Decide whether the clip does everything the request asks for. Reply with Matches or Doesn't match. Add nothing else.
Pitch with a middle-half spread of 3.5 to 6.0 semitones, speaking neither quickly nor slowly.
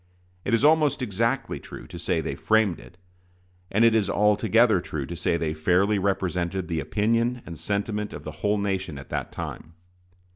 Matches